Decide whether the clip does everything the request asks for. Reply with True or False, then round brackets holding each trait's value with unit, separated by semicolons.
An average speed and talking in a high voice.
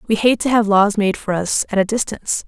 False (265 wpm; 210 Hz)